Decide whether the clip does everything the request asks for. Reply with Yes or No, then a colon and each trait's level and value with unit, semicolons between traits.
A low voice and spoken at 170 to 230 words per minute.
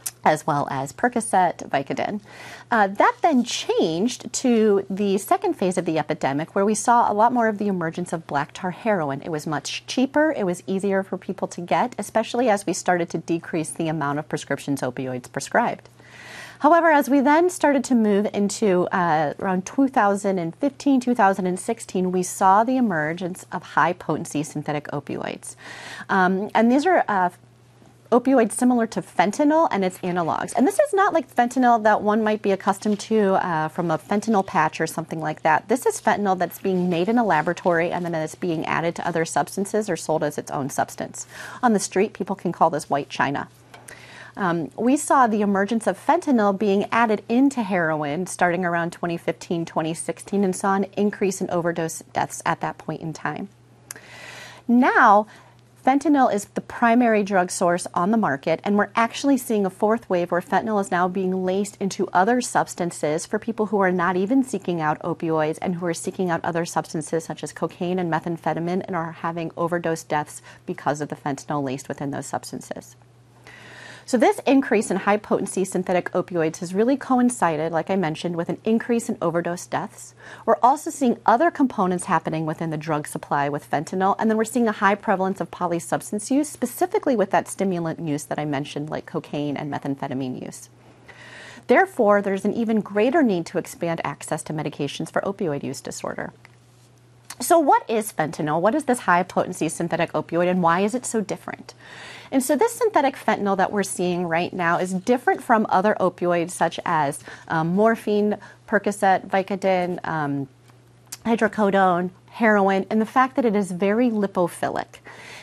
No: medium, 185 Hz; average, 180 wpm